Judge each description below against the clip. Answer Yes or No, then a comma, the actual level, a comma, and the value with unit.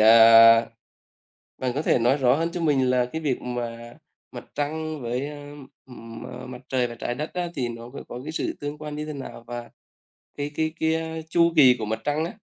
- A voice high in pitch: No, low, 135 Hz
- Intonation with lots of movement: No, average, 4.2 semitones